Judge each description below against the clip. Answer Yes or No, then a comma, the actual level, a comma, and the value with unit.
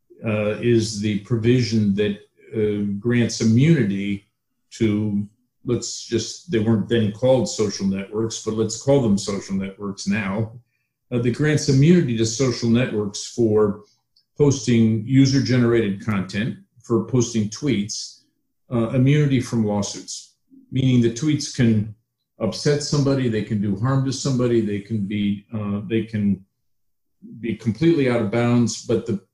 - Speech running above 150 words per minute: No, average, 140 wpm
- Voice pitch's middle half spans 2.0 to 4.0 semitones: Yes, average, 3.0 semitones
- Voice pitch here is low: Yes, low, 115 Hz